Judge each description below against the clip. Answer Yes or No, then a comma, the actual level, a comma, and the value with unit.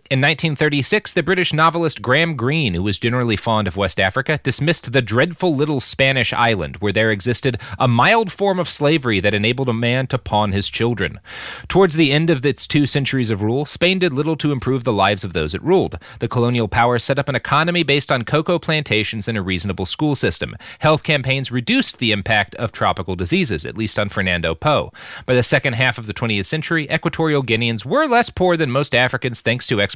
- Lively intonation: Yes, wide, 5.8 semitones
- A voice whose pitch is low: Yes, low, 130 Hz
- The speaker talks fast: Yes, fast, 210 wpm